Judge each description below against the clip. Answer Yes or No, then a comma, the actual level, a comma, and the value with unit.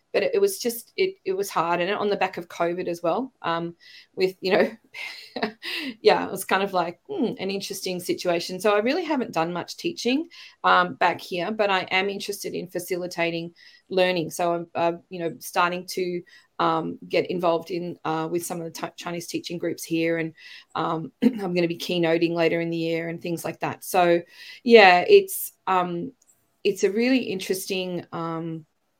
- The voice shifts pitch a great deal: No, average, 4.5 semitones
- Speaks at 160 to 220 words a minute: Yes, average, 190 wpm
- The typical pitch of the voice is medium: Yes, medium, 180 Hz